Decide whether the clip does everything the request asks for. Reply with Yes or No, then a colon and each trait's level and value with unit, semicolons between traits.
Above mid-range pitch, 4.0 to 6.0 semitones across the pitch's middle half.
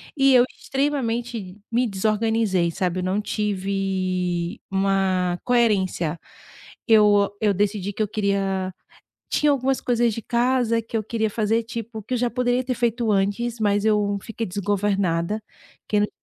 No: high, 210 Hz; average, 3.2 semitones